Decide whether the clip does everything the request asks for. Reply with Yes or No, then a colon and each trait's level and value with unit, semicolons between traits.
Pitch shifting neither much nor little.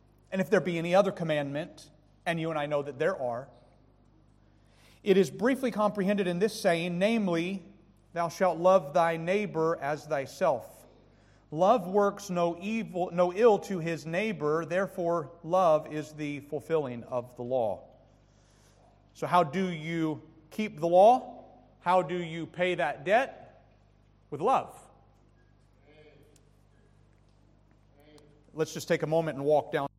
No: wide, 5.9 semitones